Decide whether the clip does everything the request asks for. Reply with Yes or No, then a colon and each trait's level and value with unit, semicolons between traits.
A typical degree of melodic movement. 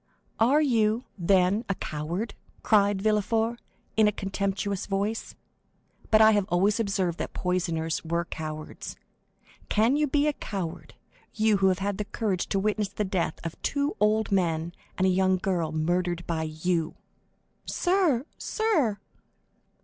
Yes: average, 3.8 semitones